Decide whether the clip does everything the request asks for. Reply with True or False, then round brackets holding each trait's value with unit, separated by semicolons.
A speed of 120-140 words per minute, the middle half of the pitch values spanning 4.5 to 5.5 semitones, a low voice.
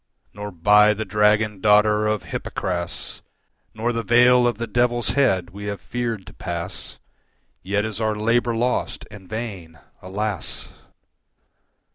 False (135 wpm; 2.8 semitones; 105 Hz)